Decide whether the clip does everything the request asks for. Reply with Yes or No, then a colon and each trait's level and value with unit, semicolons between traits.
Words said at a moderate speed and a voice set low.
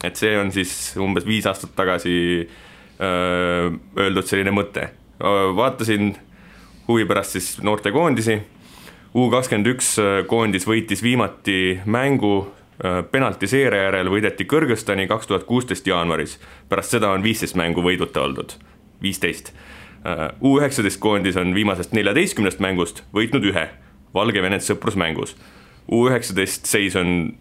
No: slow, 110 wpm; low, 100 Hz